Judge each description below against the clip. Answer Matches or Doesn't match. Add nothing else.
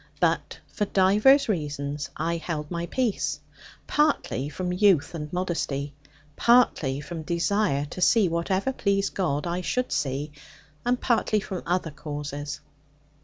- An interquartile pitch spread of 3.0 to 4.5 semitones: Doesn't match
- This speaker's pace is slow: Matches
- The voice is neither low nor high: Matches